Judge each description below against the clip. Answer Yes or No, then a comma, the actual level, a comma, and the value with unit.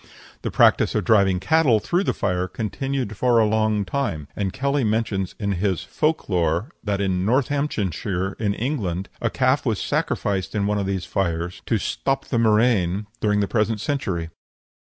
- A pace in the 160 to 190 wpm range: Yes, average, 165 wpm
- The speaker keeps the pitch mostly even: No, average, 4.0 semitones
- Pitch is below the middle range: Yes, low, 105 Hz